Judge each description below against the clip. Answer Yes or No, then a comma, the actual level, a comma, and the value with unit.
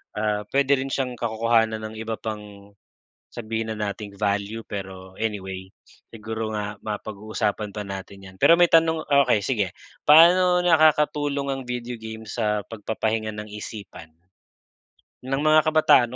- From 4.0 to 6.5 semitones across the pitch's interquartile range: Yes, average, 4.4 semitones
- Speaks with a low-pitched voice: Yes, low, 110 Hz